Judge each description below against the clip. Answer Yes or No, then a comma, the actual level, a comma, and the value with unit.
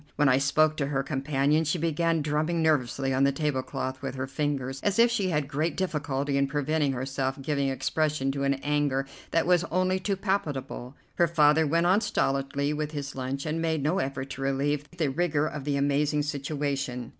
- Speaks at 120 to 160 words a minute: No, average, 190 wpm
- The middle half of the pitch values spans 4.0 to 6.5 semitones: No, narrow, 2.5 semitones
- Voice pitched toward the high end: No, medium, 145 Hz